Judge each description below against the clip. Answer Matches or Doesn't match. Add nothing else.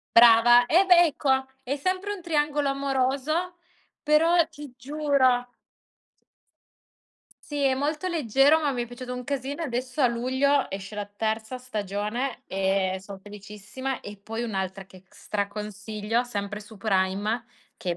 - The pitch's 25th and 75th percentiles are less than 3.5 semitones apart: Doesn't match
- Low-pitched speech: Doesn't match